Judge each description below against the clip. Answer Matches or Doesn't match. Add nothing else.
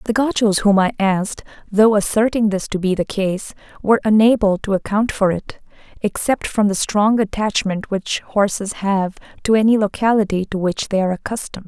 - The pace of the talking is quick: Doesn't match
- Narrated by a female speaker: Matches